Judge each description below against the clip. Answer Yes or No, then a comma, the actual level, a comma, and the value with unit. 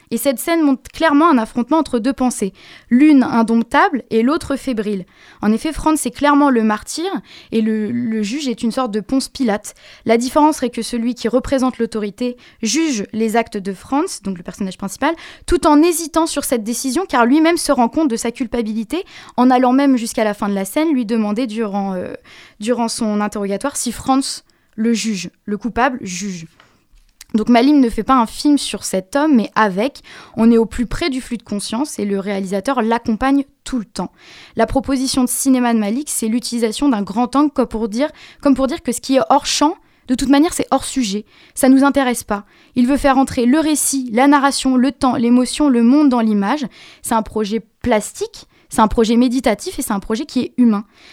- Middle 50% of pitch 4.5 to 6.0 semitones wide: No, average, 3.7 semitones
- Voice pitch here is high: Yes, high, 245 Hz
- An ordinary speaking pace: Yes, average, 210 wpm